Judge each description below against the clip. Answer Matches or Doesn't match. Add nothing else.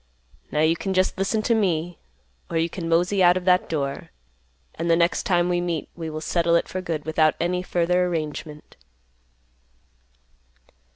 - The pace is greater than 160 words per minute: Matches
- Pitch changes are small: Matches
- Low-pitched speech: Doesn't match